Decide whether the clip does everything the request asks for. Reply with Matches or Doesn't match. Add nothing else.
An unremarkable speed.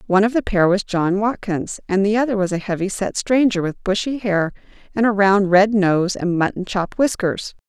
Doesn't match